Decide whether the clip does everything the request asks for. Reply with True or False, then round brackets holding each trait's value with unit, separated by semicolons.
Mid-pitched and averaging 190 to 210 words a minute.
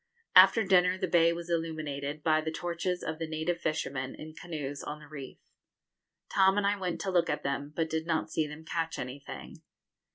True (160 Hz; 195 wpm)